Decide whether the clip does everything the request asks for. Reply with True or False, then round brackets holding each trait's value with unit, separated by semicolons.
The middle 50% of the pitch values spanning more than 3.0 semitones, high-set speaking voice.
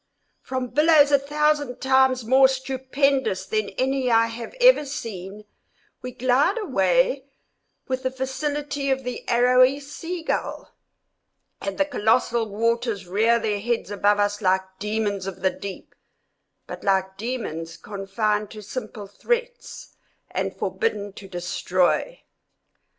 True (5.1 semitones; 240 Hz)